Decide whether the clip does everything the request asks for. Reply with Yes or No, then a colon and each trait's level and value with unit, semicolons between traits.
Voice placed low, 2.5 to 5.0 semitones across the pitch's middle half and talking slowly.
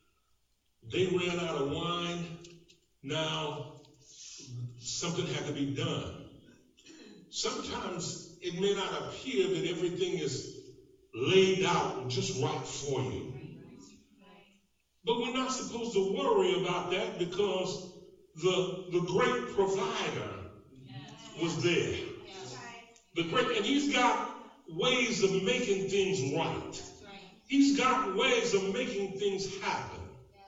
No: medium, 185 Hz; average, 4.0 semitones; slow, 110 wpm